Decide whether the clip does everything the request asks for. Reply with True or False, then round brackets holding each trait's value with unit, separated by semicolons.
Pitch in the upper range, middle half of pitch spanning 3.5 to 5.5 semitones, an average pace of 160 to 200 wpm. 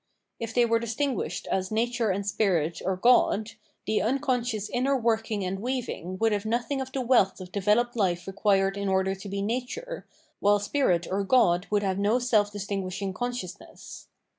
True (210 Hz; 3.9 semitones; 170 wpm)